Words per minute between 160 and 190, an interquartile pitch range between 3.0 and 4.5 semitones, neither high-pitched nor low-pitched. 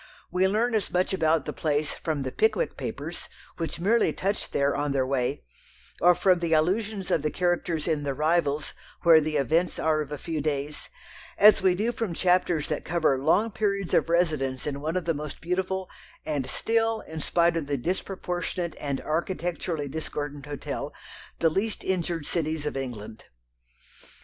Yes: average, 175 wpm; average, 3.8 semitones; medium, 165 Hz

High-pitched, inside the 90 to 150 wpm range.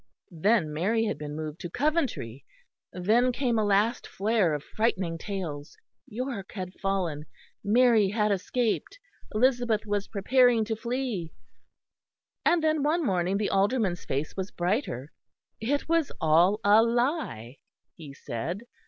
Yes: high, 205 Hz; slow, 135 wpm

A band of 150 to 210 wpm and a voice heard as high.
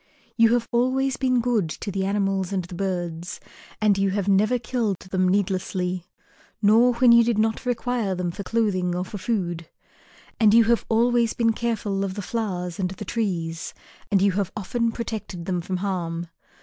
Yes: average, 180 wpm; high, 200 Hz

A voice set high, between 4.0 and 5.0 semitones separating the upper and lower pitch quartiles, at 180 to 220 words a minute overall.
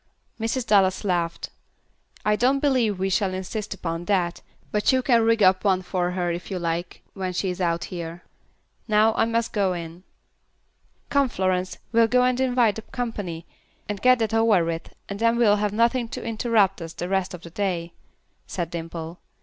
Yes: high, 195 Hz; average, 4.3 semitones; average, 185 wpm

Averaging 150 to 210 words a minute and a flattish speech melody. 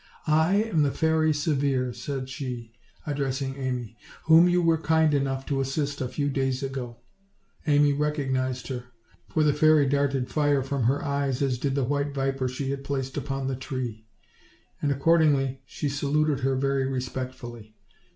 Yes: average, 165 wpm; narrow, 2.0 semitones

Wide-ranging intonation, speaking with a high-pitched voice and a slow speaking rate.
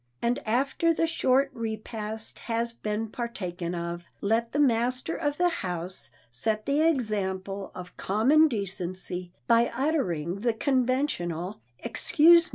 Yes: wide, 6.1 semitones; high, 225 Hz; slow, 130 wpm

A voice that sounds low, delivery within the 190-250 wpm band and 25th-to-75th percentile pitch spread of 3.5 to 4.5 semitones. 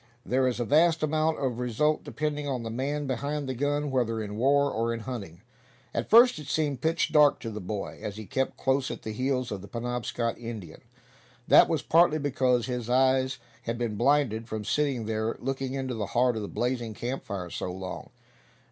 Yes: low, 125 Hz; average, 200 wpm; average, 4.0 semitones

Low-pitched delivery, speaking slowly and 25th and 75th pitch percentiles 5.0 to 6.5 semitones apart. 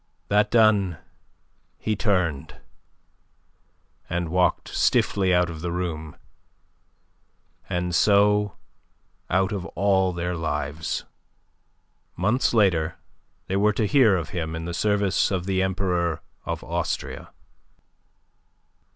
No: very low, 90 Hz; slow, 110 wpm; average, 3.0 semitones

